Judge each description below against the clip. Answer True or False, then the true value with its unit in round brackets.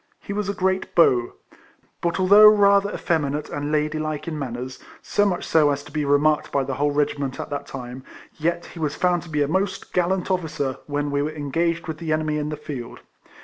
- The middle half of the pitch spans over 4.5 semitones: False (3.4 semitones)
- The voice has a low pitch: False (155 Hz)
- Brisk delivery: True (210 wpm)